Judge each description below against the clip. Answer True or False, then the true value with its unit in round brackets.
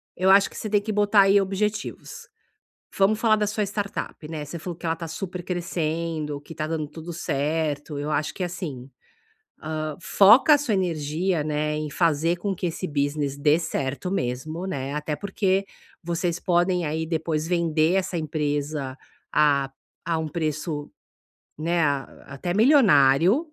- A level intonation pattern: False (4.1 semitones)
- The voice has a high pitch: False (165 Hz)